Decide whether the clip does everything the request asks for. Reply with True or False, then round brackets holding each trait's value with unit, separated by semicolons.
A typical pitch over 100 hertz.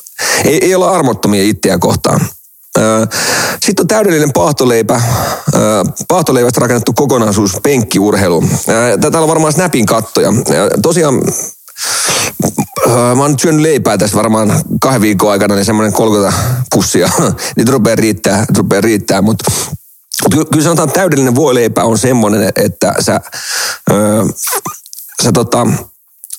True (120 Hz)